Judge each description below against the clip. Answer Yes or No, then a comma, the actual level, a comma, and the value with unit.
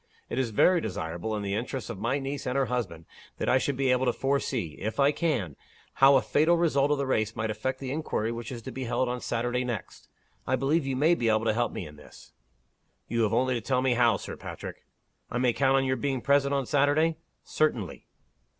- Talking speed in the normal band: No, fast, 230 wpm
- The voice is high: No, low, 130 Hz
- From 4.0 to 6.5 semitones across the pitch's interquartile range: No, average, 3.3 semitones